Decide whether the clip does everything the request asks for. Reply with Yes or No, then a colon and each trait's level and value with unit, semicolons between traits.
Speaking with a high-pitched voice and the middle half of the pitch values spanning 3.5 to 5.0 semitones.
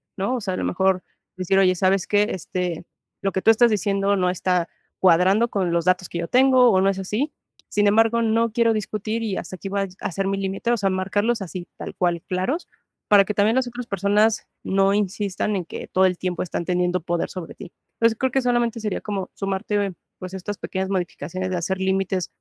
No: high, 195 Hz; average, 2.7 semitones